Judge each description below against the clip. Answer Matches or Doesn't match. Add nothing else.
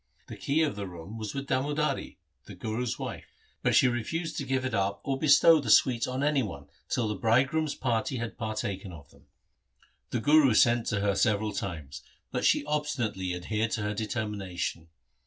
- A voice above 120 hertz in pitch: Doesn't match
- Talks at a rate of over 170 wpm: Matches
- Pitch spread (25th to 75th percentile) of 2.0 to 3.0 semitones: Doesn't match